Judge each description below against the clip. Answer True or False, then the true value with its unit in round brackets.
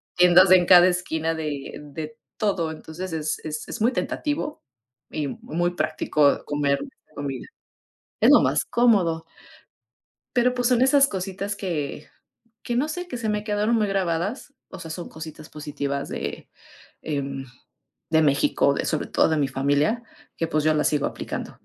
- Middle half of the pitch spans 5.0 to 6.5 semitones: True (5.6 semitones)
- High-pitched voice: False (165 Hz)